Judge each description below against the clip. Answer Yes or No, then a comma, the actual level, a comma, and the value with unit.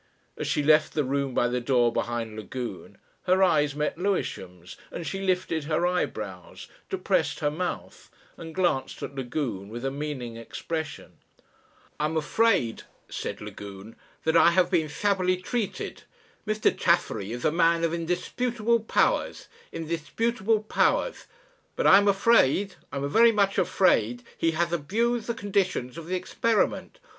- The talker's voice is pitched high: No, medium, 165 Hz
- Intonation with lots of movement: Yes, wide, 6.6 semitones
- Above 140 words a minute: Yes, average, 150 wpm